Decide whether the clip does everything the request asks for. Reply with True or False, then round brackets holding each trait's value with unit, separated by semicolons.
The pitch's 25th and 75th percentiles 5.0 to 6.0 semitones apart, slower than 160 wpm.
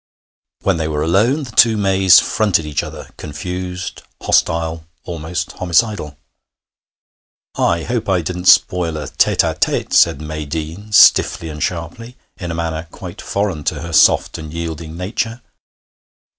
False (3.5 semitones; 145 wpm)